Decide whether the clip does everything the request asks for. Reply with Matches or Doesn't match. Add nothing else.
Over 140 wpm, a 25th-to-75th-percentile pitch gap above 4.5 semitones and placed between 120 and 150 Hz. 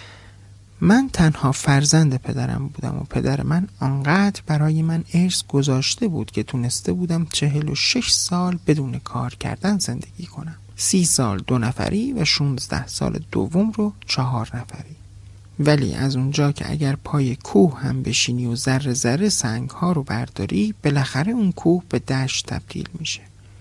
Matches